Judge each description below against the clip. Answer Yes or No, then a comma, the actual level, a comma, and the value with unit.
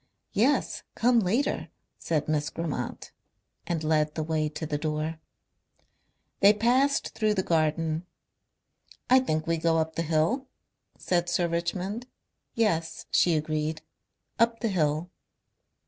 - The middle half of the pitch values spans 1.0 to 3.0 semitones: No, average, 5.2 semitones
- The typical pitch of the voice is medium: Yes, medium, 165 Hz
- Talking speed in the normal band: No, slow, 130 wpm